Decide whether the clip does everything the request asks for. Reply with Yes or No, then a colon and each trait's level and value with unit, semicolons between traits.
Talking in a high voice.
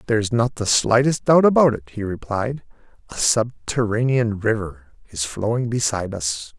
No: low, 115 Hz